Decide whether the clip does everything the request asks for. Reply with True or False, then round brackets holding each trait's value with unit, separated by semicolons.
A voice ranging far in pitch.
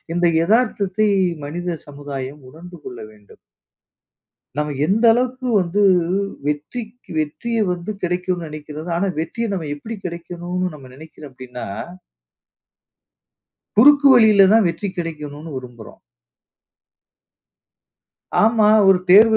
True (6.3 semitones)